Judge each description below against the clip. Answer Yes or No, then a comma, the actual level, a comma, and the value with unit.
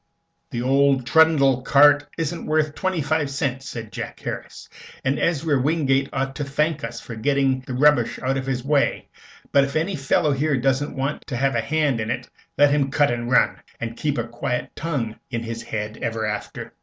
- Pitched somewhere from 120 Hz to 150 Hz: Yes, low, 135 Hz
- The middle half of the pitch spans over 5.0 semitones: No, average, 3.1 semitones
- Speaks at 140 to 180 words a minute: No, average, 195 wpm